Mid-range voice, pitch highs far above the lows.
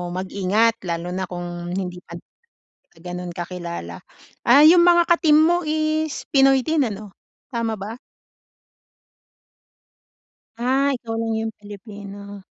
No: high, 215 Hz; wide, 7.4 semitones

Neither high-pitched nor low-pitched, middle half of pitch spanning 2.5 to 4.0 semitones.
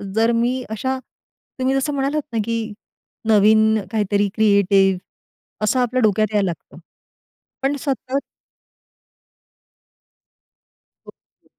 No: high, 220 Hz; average, 3.7 semitones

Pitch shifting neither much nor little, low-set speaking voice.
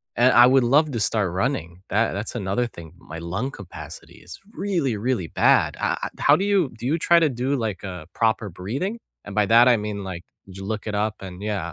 Yes: average, 4.9 semitones; low, 110 Hz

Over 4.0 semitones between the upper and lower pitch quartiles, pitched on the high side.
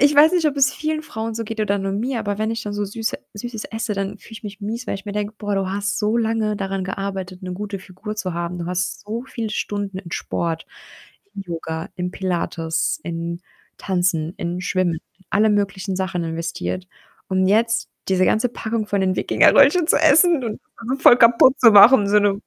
No: average, 3.4 semitones; high, 205 Hz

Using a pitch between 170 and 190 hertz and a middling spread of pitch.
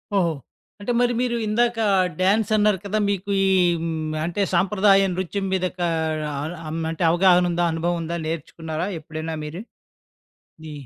Yes: medium, 185 Hz; average, 3.6 semitones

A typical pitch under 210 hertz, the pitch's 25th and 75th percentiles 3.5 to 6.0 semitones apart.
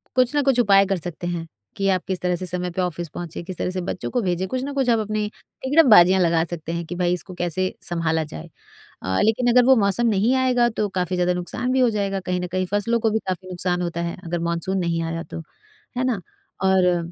Yes: medium, 185 Hz; average, 3.9 semitones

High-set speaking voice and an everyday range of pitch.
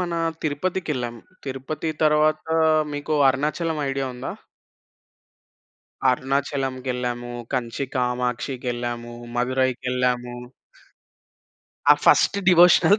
No: low, 130 Hz; average, 3.6 semitones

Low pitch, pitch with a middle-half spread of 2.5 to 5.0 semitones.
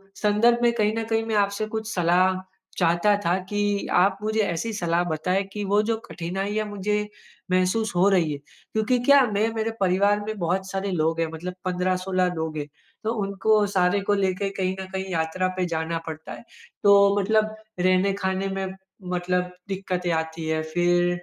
No: high, 190 Hz; average, 2.8 semitones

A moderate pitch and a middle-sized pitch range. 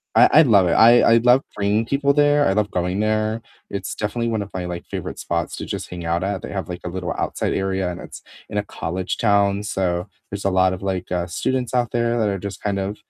No: low, 100 Hz; average, 3.5 semitones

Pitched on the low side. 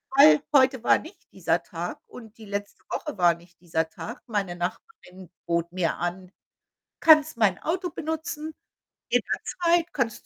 No: high, 215 Hz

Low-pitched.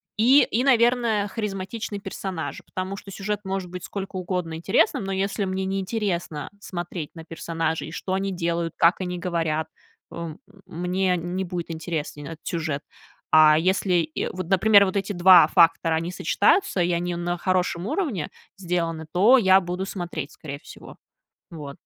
No: medium, 180 Hz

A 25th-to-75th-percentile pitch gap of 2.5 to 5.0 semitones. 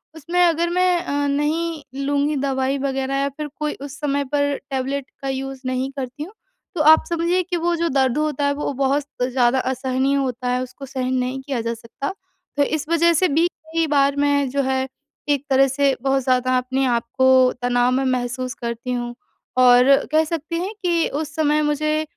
Yes: average, 2.9 semitones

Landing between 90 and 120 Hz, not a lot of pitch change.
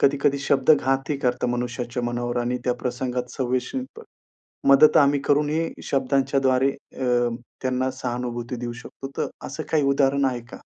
No: low, 130 Hz; narrow, 2.2 semitones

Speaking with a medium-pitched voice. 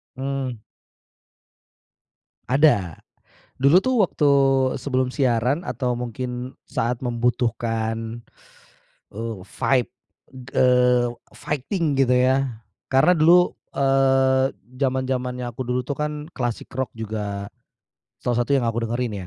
No: low, 125 Hz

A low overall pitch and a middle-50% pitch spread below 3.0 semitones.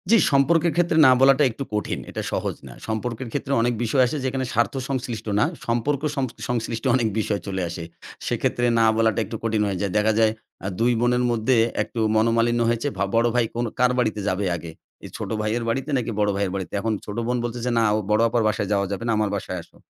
Yes: low, 115 Hz; narrow, 2.6 semitones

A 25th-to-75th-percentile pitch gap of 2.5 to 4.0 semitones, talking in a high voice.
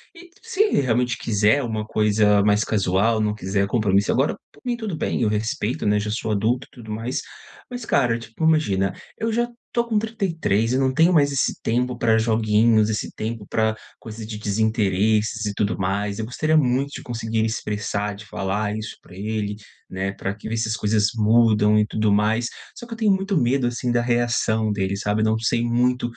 No: average, 2.9 semitones; low, 110 Hz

